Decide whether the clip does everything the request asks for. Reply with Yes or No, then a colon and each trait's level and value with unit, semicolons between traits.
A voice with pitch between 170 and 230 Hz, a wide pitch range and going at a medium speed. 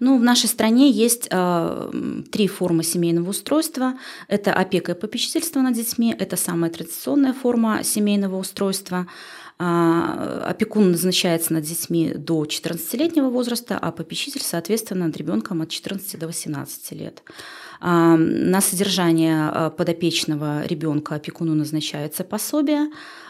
Yes: medium, 185 Hz; wide, 6.3 semitones; average, 125 wpm